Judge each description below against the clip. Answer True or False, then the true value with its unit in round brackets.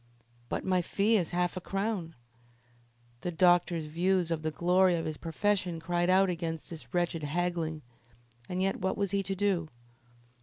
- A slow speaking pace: False (165 wpm)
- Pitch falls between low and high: True (175 Hz)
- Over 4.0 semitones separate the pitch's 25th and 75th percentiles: False (2.4 semitones)